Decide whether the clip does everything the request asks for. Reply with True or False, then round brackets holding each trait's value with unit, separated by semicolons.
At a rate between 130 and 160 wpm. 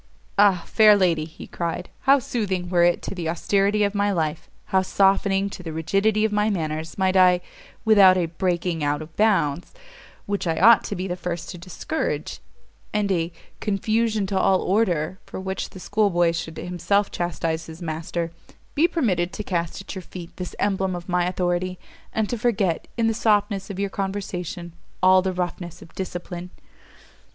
False (180 wpm)